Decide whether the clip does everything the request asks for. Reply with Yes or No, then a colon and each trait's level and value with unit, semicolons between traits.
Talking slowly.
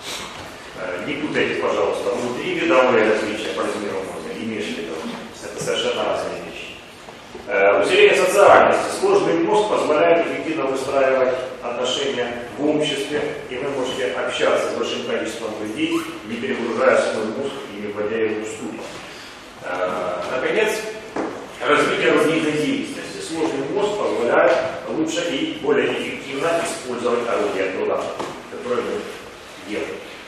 No: average, 120 wpm